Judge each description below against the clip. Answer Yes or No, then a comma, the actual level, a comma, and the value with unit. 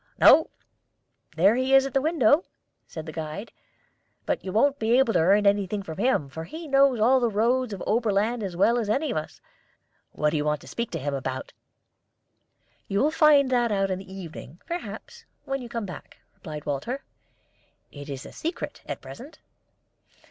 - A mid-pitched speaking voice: No, high, 215 Hz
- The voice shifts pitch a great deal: Yes, wide, 7.6 semitones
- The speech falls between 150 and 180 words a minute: No, average, 190 wpm